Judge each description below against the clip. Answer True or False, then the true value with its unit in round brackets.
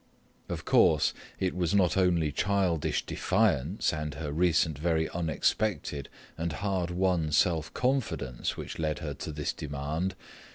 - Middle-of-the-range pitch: False (80 Hz)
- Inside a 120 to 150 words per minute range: True (135 wpm)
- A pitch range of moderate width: True (3.2 semitones)